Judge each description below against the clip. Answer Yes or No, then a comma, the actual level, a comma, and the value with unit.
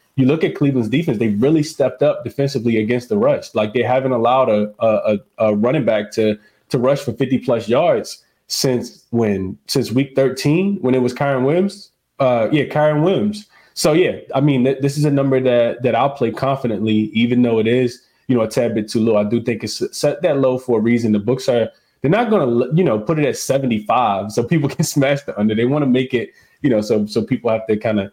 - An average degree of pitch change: Yes, average, 3.7 semitones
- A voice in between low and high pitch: No, low, 125 Hz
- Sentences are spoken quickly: Yes, fast, 235 wpm